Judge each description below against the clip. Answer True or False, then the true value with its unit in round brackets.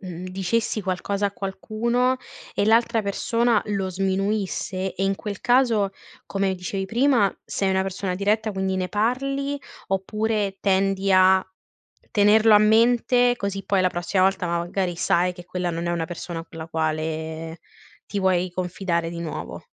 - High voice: True (195 Hz)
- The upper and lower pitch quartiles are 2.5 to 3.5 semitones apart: True (2.9 semitones)